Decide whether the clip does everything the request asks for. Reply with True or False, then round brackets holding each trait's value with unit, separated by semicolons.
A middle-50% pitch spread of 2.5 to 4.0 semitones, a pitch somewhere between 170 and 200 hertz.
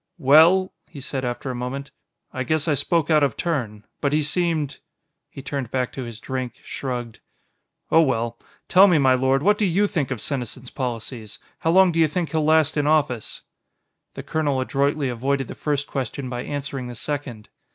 False (3.7 semitones; 140 Hz)